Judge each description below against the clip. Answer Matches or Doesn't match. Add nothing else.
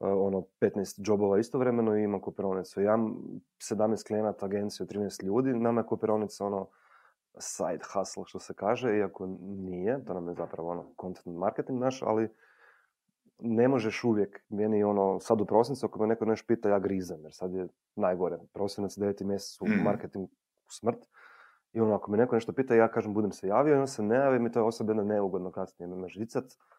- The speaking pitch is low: Matches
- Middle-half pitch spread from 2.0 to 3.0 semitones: Matches